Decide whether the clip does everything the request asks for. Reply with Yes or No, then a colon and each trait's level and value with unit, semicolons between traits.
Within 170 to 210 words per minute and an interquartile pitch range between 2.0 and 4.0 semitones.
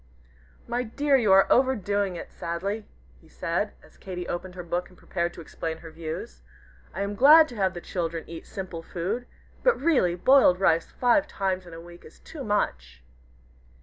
No: average, 180 wpm; average, 5.2 semitones